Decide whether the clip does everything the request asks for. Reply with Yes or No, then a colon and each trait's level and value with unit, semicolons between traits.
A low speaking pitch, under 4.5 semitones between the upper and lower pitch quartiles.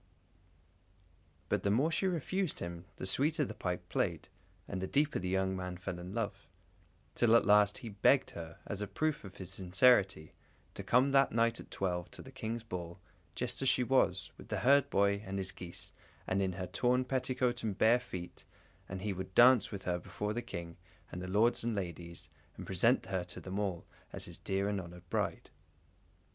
No: low, 100 Hz; average, 4.8 semitones